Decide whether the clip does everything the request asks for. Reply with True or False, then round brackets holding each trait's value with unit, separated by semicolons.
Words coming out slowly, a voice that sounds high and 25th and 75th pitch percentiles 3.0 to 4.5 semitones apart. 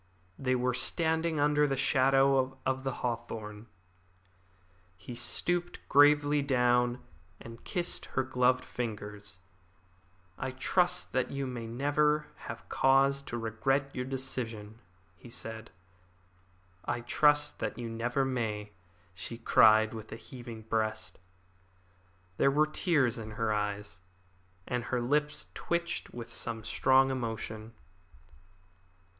False (120 wpm; 125 Hz; 3.5 semitones)